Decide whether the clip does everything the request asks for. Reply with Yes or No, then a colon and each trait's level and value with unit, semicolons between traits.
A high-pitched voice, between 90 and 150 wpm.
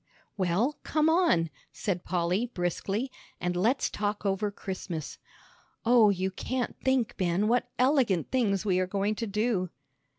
Yes: high, 205 Hz; average, 140 wpm